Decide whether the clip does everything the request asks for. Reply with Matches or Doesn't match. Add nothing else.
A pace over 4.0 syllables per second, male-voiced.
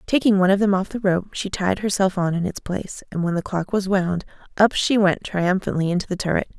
Doesn't match